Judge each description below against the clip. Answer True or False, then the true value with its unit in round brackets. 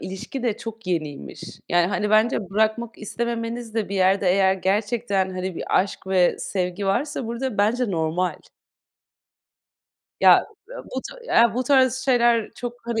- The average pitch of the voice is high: True (215 Hz)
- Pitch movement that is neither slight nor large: True (3.8 semitones)